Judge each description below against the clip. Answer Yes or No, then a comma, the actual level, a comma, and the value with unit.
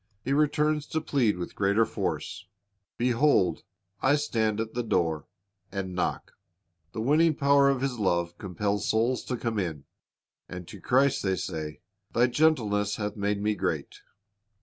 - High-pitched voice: No, low, 110 Hz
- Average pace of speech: Yes, average, 150 wpm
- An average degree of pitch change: No, wide, 6.0 semitones